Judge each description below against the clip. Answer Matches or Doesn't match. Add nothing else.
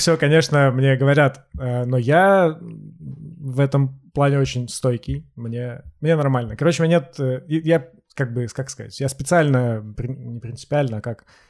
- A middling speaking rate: Matches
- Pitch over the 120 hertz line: Matches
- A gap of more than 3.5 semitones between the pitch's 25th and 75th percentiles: Matches